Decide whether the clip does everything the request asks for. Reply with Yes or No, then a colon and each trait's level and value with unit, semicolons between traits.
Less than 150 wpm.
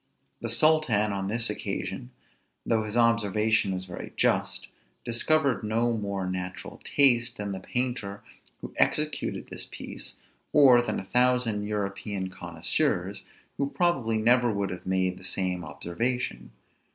Yes: slow, 135 wpm